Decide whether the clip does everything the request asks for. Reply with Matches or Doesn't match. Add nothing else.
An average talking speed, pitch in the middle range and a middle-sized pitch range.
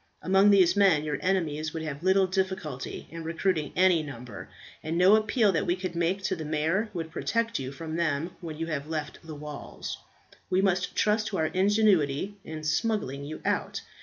Matches